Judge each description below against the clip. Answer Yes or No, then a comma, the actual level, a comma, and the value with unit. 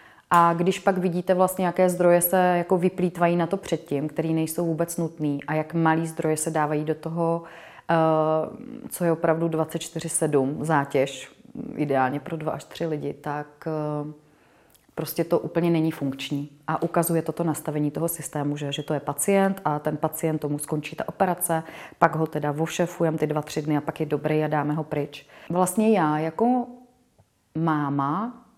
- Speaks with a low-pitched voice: No, medium, 160 Hz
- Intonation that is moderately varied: No, narrow, 2.3 semitones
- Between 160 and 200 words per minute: Yes, fast, 170 wpm